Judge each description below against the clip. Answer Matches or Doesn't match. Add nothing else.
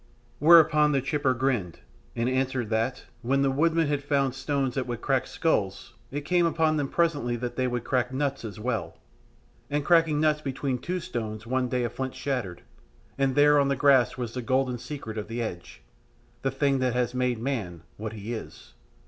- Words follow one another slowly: Doesn't match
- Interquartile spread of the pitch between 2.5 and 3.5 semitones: Matches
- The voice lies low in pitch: Matches